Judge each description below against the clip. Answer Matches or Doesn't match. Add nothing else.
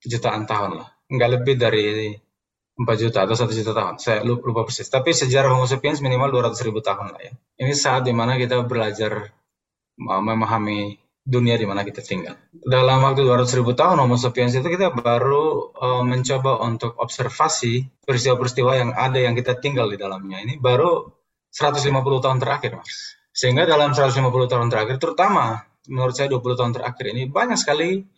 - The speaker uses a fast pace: Matches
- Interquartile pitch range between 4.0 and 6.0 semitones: Doesn't match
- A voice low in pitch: Matches